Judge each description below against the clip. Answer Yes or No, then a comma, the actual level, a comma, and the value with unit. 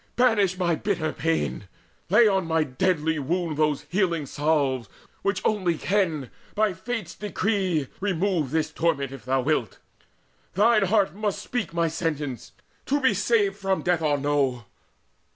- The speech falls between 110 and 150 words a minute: Yes, average, 145 wpm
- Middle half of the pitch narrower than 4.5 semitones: No, average, 5.0 semitones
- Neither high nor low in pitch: Yes, medium, 170 Hz